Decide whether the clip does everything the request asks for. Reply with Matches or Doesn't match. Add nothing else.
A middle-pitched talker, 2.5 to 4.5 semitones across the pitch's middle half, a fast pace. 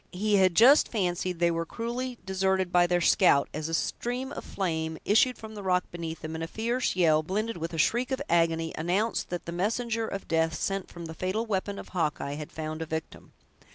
Doesn't match